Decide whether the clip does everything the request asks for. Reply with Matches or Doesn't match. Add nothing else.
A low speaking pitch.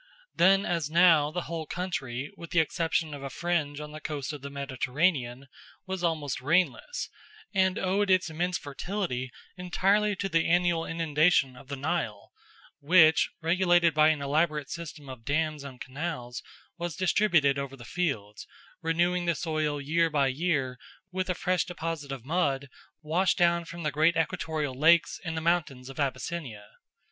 Doesn't match